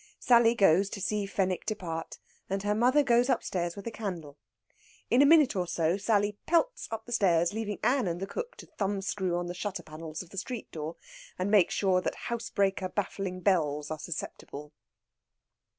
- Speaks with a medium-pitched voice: No, high, 195 Hz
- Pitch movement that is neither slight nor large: Yes, average, 4.2 semitones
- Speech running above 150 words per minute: Yes, average, 180 wpm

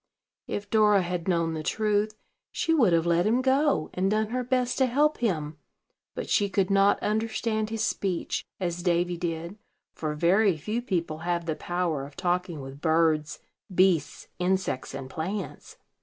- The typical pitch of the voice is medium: Yes, medium, 180 Hz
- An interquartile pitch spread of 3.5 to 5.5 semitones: Yes, average, 4.5 semitones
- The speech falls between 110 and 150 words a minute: No, average, 165 wpm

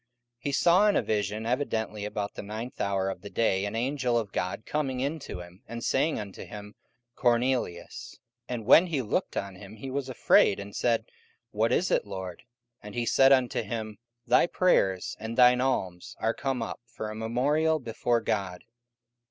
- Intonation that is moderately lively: Yes, average, 4.2 semitones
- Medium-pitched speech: No, low, 115 Hz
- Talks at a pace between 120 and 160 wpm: No, average, 190 wpm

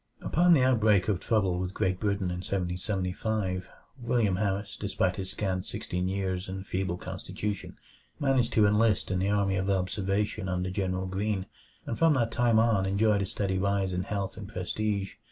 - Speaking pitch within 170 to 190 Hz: No, low, 100 Hz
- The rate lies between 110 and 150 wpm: No, average, 170 wpm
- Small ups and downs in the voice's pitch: Yes, narrow, 2.3 semitones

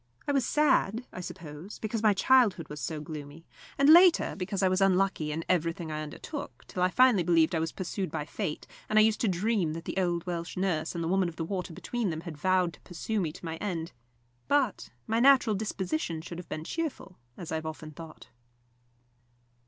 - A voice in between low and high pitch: Yes, medium, 180 Hz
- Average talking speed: No, fast, 210 wpm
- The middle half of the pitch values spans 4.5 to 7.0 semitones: Yes, average, 4.8 semitones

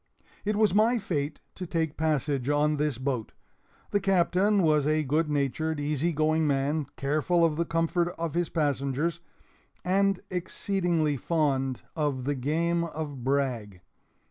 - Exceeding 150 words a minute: No, average, 145 wpm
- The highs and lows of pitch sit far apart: No, average, 3.3 semitones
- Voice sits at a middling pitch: Yes, medium, 155 Hz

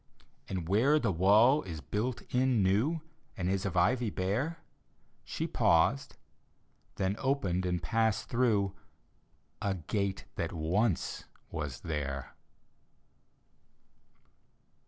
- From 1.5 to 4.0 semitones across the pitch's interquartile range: No, average, 5.2 semitones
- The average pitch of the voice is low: Yes, low, 100 Hz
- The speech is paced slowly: Yes, slow, 110 wpm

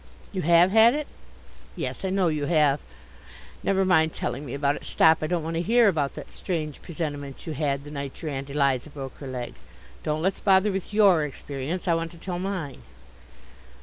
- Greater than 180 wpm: Yes, average, 200 wpm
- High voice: No, medium, 160 Hz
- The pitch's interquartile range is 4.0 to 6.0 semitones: Yes, average, 4.7 semitones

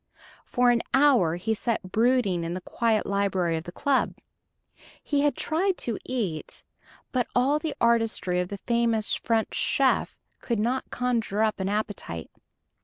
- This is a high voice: Yes, high, 225 Hz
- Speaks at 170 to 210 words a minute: No, average, 155 wpm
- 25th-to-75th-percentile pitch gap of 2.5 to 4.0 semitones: No, average, 4.5 semitones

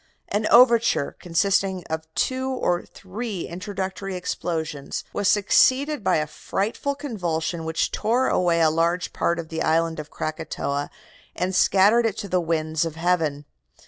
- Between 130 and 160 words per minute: Yes, average, 145 wpm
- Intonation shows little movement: No, average, 4.3 semitones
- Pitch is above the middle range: No, medium, 180 Hz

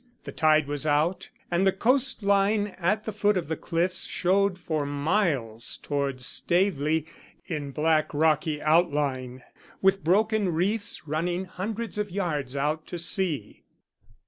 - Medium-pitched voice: Yes, medium, 170 Hz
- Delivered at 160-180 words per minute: No, slow, 135 wpm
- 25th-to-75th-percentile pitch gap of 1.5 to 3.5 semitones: No, average, 4.7 semitones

